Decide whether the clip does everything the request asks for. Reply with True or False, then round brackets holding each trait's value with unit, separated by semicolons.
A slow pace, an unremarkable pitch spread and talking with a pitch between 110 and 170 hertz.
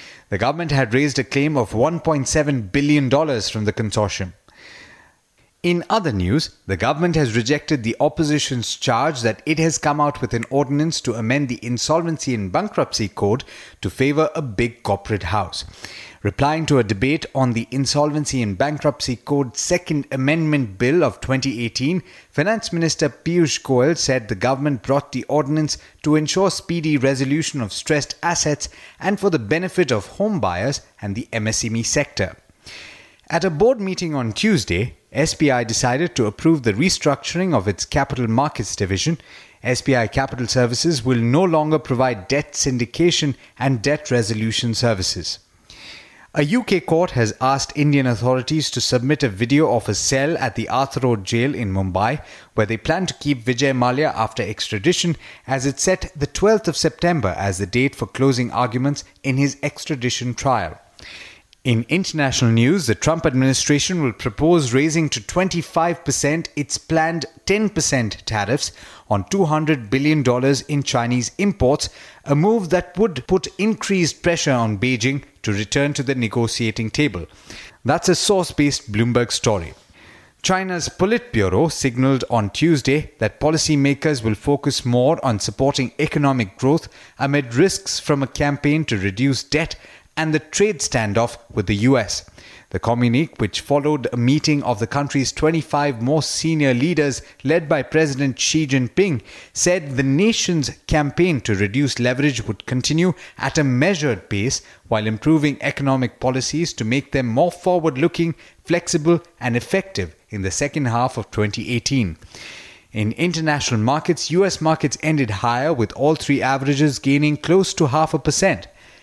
False (150 wpm; 4.7 semitones; 140 Hz)